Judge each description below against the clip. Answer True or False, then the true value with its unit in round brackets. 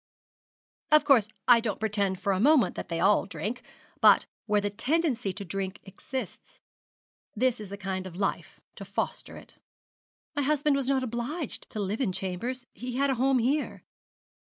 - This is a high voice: True (230 Hz)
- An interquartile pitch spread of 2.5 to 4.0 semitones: False (5.2 semitones)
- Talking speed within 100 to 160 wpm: False (175 wpm)